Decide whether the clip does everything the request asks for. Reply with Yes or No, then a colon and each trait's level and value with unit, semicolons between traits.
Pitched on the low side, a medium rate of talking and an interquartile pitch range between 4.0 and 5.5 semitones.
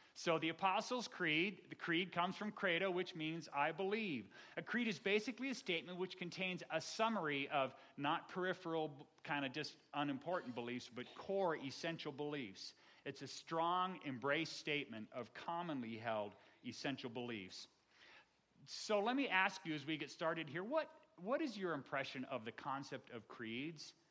No: medium, 160 Hz; average, 160 wpm; average, 4.8 semitones